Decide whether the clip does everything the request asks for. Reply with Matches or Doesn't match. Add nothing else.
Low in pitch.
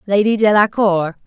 Doesn't match